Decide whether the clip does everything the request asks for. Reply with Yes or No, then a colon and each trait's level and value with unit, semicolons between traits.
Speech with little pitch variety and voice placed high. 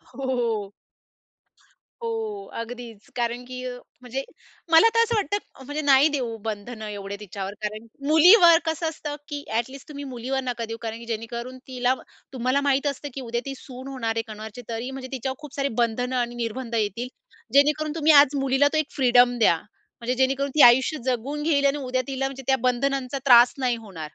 No: average, 3.3 semitones; very high, 255 Hz